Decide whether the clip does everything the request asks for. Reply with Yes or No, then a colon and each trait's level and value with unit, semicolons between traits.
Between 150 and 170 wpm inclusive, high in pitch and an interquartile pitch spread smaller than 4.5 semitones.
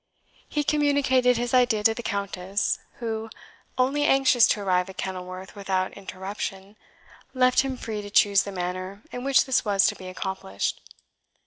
No: average, 155 wpm; high, 205 Hz; average, 4.8 semitones